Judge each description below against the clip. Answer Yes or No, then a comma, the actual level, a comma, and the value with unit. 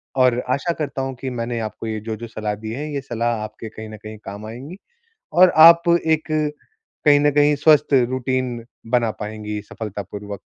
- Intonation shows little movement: No, average, 5.2 semitones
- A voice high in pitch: No, low, 125 Hz